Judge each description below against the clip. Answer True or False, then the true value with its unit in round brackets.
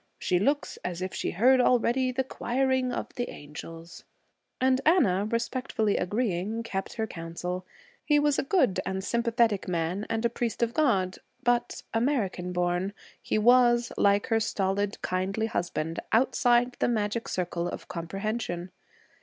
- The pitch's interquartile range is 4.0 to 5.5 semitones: True (4.9 semitones)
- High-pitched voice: True (220 Hz)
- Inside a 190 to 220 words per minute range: False (145 wpm)